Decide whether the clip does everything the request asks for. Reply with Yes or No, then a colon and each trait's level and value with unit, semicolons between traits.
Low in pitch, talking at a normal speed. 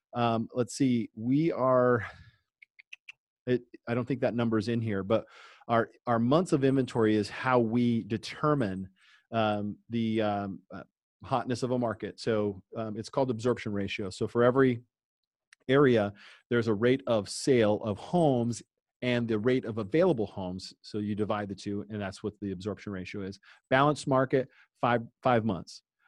Yes: low, 115 Hz; average, 165 wpm